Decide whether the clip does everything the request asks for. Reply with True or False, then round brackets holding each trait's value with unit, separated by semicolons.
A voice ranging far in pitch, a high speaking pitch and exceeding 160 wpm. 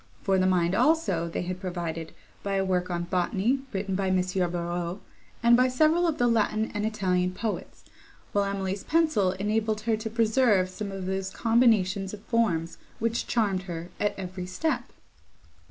False (3.6 semitones; 195 Hz; 170 wpm)